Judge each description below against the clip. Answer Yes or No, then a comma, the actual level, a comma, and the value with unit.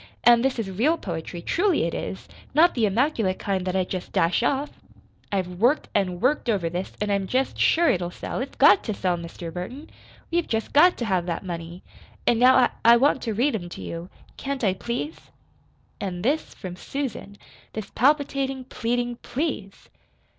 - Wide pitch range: Yes, wide, 6.5 semitones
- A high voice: Yes, high, 220 Hz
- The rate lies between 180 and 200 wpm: Yes, average, 185 wpm